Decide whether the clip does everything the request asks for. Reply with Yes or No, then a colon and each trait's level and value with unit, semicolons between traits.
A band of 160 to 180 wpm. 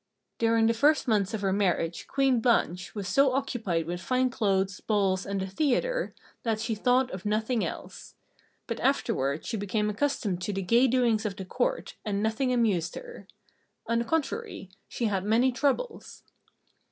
Yes: average, 170 wpm